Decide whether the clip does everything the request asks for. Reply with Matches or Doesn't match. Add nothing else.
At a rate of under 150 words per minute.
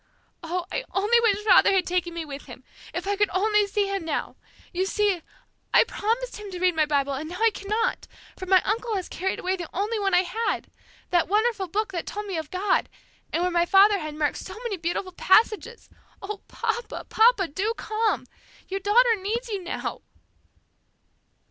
Doesn't match